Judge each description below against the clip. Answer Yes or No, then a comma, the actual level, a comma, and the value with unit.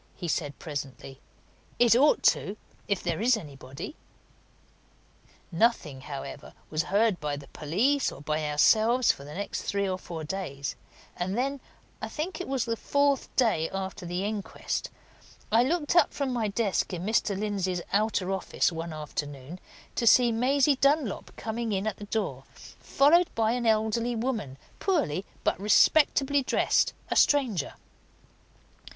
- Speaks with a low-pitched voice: No, high, 210 Hz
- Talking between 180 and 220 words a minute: No, average, 150 wpm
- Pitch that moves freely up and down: Yes, wide, 7.0 semitones